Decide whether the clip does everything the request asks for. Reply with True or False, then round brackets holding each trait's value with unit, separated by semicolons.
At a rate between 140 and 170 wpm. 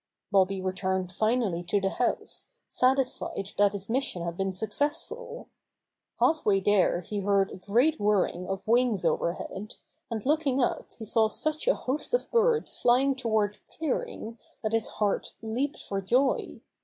True (160 wpm)